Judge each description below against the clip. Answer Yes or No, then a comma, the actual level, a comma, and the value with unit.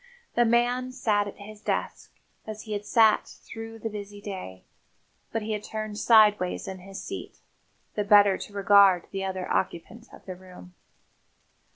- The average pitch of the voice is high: Yes, high, 205 Hz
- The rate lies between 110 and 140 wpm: No, average, 165 wpm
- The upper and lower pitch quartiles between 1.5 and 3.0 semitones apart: Yes, narrow, 2.4 semitones